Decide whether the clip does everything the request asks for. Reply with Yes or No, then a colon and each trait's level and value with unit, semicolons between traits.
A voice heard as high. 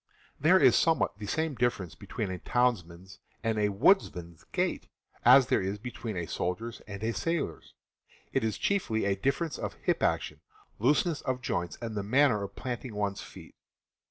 No: low, 110 Hz